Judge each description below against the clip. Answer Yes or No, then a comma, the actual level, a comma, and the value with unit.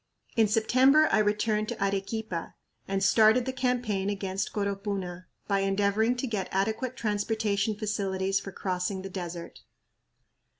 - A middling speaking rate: No, slow, 130 wpm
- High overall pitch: Yes, high, 205 Hz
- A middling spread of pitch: No, narrow, 2.3 semitones